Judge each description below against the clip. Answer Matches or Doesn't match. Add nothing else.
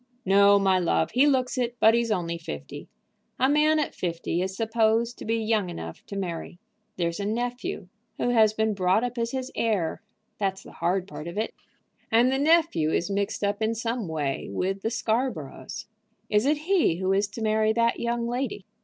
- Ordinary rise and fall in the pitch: Matches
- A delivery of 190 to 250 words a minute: Matches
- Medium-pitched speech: Doesn't match